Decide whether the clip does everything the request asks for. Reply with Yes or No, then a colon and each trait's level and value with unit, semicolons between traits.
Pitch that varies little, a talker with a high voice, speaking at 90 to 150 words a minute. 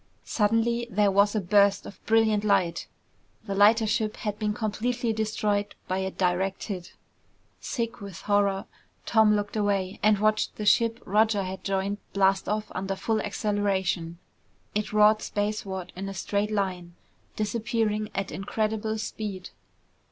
Yes: narrow, 1.8 semitones; high, 205 Hz; average, 145 wpm